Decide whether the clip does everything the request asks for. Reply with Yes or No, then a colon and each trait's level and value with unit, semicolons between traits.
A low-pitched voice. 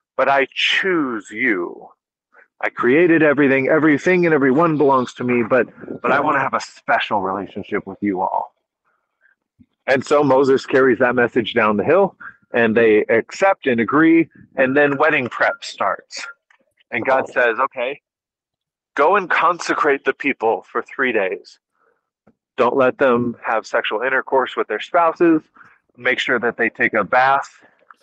No: medium, 155 Hz